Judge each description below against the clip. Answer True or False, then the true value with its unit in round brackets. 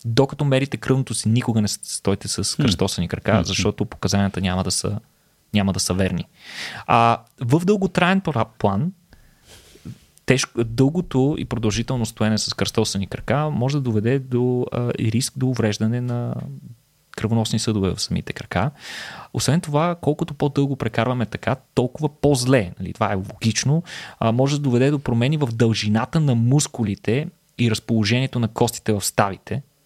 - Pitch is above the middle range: False (120 Hz)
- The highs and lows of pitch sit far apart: False (4.2 semitones)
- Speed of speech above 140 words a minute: True (150 wpm)